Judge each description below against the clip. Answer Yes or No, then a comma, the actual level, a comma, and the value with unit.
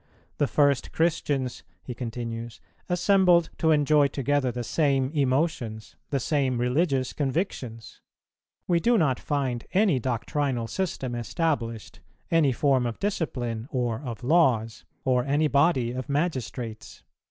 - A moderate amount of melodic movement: Yes, average, 4.3 semitones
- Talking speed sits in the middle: No, slow, 125 wpm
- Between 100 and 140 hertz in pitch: Yes, low, 135 Hz